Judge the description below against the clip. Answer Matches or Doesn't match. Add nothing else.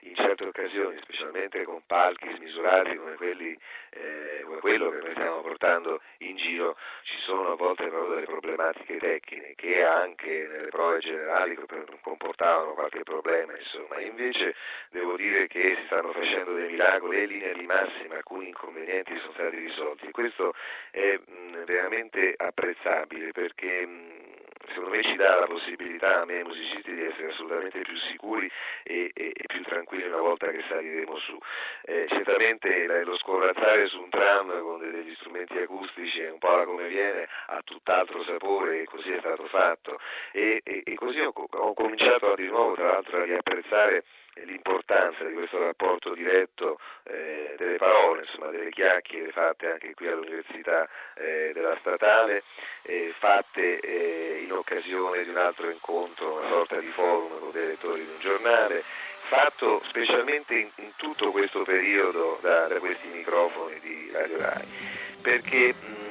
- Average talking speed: Matches